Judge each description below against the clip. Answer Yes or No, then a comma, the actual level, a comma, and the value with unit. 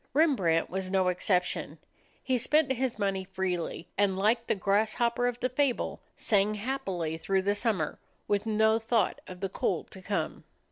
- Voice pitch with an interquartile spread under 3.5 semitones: No, average, 3.9 semitones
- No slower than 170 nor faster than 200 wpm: No, average, 160 wpm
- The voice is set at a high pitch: Yes, high, 205 Hz